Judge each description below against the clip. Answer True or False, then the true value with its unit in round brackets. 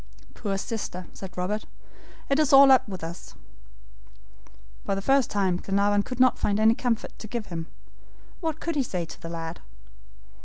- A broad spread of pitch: True (5.7 semitones)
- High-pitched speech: True (205 Hz)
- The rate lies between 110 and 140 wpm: False (170 wpm)